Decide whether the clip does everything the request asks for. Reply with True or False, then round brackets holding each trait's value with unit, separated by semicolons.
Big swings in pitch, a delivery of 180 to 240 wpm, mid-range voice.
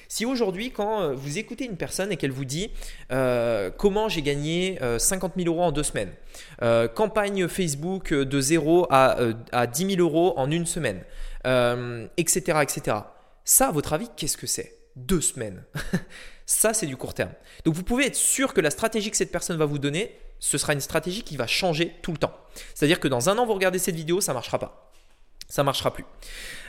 True (5.9 semitones; 210 wpm; 165 Hz)